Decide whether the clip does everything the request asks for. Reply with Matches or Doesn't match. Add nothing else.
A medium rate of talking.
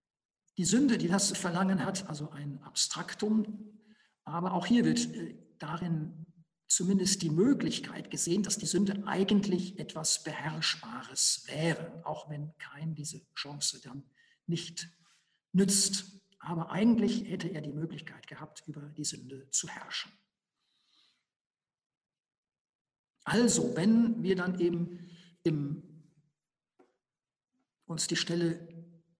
Doesn't match